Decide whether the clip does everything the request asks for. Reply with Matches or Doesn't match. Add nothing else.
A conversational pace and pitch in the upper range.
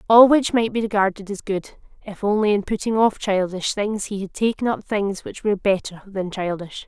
Doesn't match